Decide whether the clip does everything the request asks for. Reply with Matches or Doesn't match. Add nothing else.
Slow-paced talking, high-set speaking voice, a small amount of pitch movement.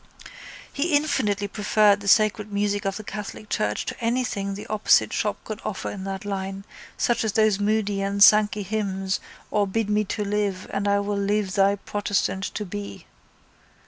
Doesn't match